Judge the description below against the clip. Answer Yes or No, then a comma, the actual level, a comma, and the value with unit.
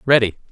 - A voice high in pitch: No, low, 115 Hz